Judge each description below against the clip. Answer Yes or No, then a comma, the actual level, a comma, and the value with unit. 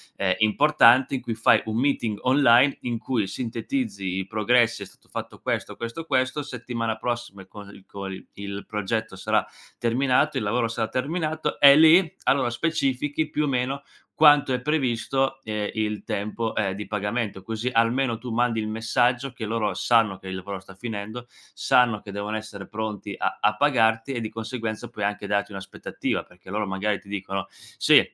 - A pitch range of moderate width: Yes, average, 3.7 semitones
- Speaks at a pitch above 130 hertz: No, low, 115 Hz